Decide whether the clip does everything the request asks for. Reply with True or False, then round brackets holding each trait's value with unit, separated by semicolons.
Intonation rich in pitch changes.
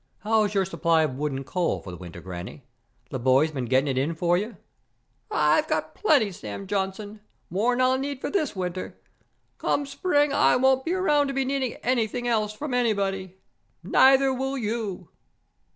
True (7.9 semitones)